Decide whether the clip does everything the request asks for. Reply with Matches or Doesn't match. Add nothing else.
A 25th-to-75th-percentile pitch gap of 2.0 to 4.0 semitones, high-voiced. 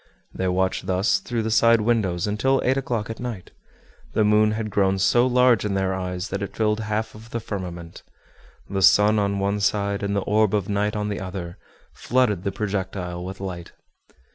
Doesn't match